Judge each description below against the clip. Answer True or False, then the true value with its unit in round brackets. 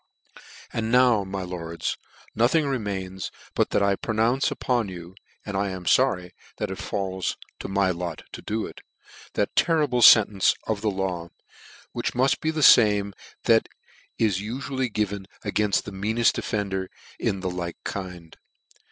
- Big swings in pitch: False (3.3 semitones)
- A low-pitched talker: True (100 Hz)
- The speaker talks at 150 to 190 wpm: True (155 wpm)